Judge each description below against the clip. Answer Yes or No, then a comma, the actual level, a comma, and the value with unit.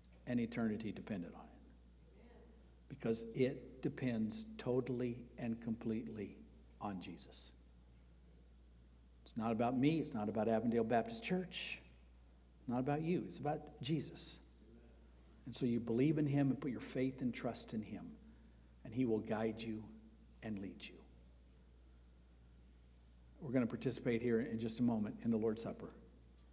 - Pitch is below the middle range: Yes, low, 110 Hz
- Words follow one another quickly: No, average, 145 wpm